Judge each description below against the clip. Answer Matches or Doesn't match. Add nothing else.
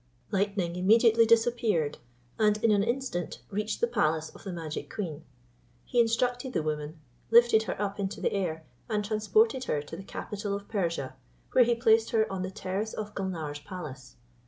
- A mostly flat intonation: Doesn't match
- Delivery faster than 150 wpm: Matches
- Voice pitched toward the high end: Matches